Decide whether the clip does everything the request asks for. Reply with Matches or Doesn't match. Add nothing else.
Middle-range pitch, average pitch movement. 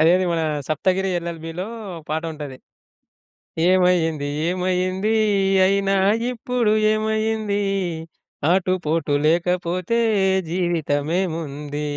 Matches